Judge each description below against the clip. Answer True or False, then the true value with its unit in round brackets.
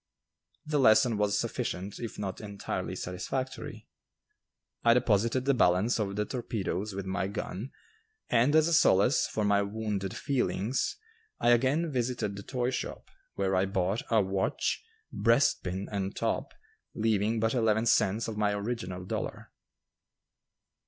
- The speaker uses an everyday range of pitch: True (3.6 semitones)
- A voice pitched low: True (110 Hz)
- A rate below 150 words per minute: True (140 wpm)